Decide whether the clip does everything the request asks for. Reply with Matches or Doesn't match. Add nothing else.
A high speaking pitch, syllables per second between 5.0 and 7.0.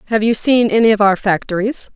Matches